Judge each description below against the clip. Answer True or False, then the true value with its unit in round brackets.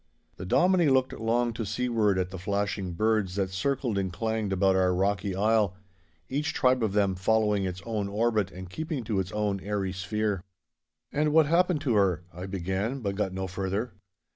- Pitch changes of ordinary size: True (3.5 semitones)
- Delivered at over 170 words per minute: True (185 wpm)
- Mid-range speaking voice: False (105 Hz)